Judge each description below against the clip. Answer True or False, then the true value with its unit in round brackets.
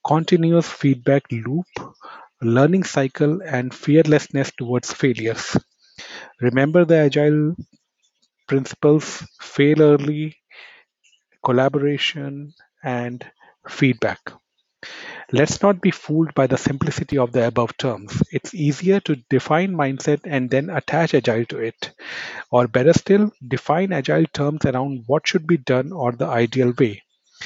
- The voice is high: False (140 Hz)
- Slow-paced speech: True (120 wpm)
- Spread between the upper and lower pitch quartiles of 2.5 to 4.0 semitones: True (3.4 semitones)